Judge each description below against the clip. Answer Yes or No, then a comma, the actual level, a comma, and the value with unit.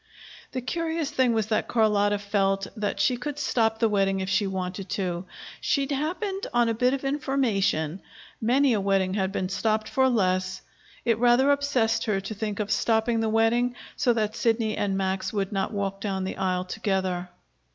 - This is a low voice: No, high, 215 Hz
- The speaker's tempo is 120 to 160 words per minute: No, average, 185 wpm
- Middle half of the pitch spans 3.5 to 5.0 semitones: Yes, average, 3.9 semitones